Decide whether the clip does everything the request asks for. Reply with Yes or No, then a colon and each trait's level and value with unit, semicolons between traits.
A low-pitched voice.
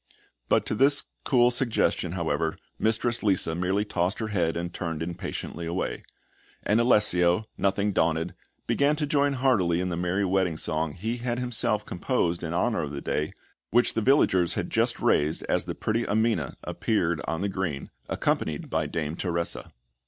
Yes: very low, 95 Hz